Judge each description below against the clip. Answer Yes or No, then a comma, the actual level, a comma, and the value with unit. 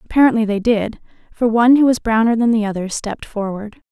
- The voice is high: Yes, high, 225 Hz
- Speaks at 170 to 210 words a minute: Yes, average, 200 wpm